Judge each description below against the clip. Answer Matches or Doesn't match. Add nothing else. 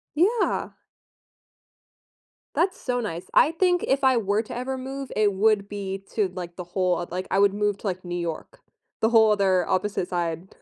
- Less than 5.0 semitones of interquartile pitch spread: Doesn't match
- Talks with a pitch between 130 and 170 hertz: Doesn't match